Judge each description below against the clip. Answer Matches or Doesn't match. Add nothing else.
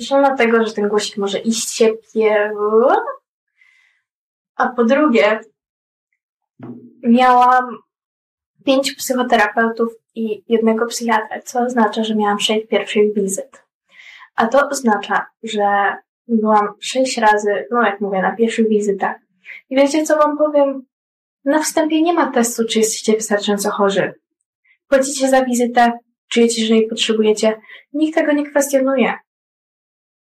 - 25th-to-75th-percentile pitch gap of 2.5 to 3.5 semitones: Doesn't match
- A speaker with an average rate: Matches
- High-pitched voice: Matches